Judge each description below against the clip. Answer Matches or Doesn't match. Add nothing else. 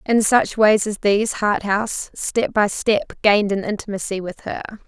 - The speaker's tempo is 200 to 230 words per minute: Doesn't match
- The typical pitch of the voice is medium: Doesn't match